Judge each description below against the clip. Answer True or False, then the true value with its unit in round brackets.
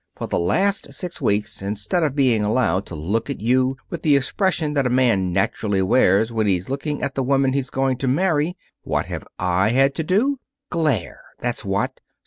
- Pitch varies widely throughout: True (6.1 semitones)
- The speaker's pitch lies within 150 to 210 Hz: False (130 Hz)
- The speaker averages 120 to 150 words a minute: False (195 wpm)